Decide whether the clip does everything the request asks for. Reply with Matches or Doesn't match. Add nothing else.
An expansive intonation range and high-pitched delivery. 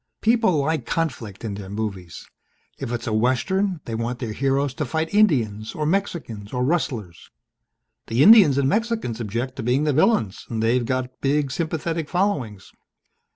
Doesn't match